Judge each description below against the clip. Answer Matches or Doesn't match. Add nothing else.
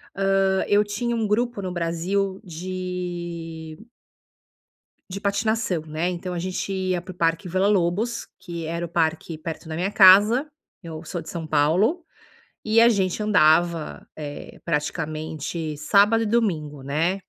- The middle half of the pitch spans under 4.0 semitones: Matches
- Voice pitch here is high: Doesn't match